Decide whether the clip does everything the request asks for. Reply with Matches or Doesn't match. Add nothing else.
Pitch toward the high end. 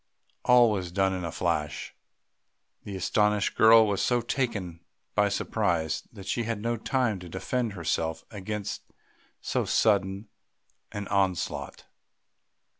Doesn't match